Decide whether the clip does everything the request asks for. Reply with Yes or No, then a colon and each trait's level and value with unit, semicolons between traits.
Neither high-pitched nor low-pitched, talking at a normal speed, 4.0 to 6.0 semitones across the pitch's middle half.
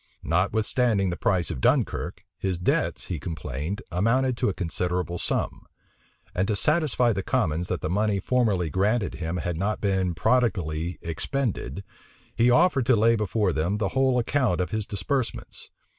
No: low, 100 Hz; average, 160 wpm; average, 4.9 semitones